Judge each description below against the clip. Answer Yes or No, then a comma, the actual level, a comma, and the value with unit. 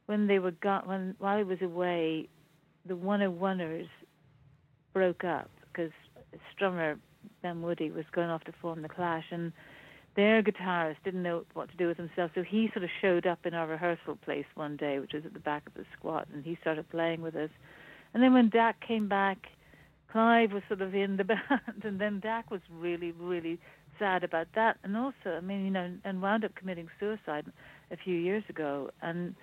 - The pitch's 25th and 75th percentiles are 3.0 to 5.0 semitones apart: Yes, average, 3.4 semitones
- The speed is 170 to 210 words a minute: Yes, fast, 205 wpm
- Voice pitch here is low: No, medium, 175 Hz